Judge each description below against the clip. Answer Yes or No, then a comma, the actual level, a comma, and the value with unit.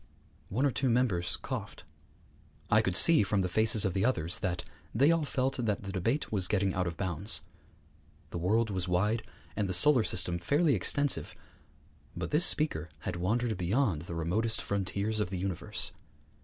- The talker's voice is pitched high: No, low, 100 Hz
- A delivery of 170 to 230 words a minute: Yes, average, 175 wpm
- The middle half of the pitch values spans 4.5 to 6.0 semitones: Yes, average, 5.2 semitones